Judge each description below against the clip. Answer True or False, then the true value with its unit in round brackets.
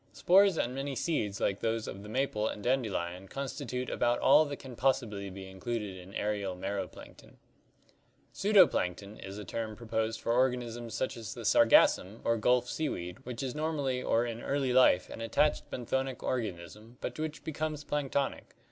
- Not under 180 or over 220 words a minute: True (185 wpm)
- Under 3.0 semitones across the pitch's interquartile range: False (4.5 semitones)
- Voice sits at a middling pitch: False (120 Hz)